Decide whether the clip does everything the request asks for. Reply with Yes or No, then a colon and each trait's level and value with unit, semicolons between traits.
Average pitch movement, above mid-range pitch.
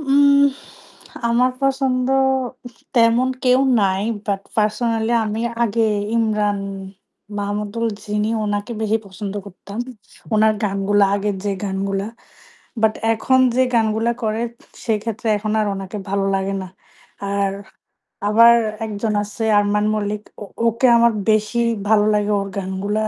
No: narrow, 2.3 semitones; high, 215 Hz